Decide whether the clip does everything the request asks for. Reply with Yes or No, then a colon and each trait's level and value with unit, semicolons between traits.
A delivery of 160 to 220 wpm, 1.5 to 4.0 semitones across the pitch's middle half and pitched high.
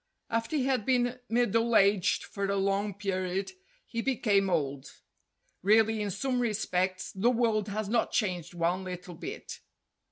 No: average, 150 wpm; average, 3.7 semitones; high, 205 Hz